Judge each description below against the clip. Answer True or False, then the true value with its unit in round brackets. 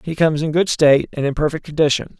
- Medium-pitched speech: True (150 Hz)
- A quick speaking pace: True (245 wpm)